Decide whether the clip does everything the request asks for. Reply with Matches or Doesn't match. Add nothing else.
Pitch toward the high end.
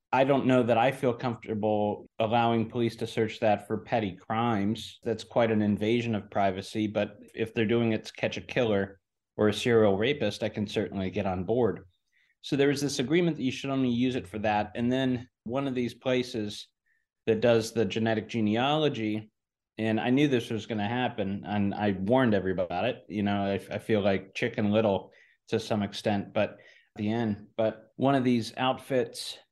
Doesn't match